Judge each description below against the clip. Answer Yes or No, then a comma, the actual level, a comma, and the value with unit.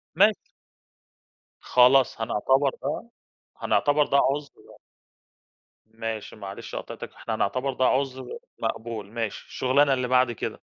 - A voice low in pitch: Yes, low, 130 Hz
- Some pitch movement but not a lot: Yes, average, 3.0 semitones